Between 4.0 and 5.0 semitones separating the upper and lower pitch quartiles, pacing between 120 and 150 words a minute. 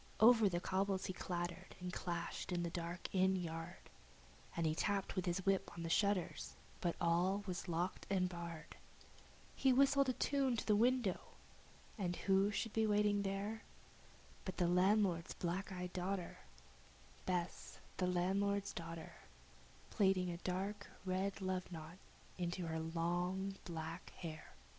No: narrow, 2.5 semitones; average, 145 wpm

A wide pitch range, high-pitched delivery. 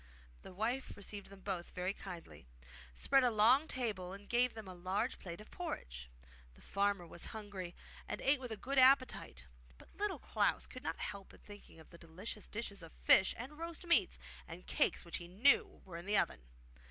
Yes: wide, 5.8 semitones; high, 205 Hz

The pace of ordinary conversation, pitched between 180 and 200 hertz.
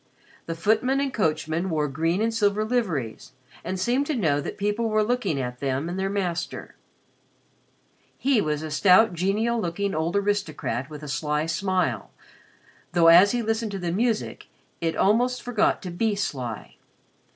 Yes: average, 160 wpm; high, 190 Hz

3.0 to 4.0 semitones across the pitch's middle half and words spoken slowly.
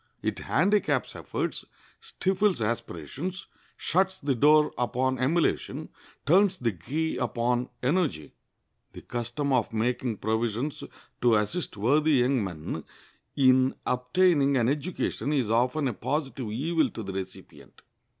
No: average, 5.0 semitones; slow, 120 wpm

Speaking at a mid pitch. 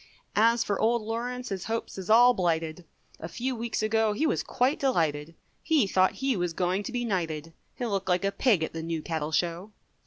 No: high, 200 Hz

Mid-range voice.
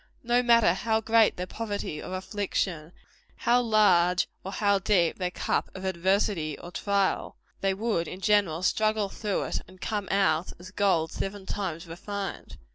No: high, 195 Hz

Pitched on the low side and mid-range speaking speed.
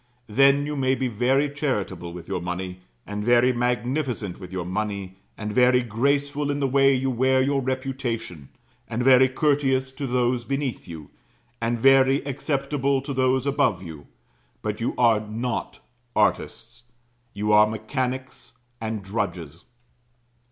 Yes: low, 125 Hz; average, 145 wpm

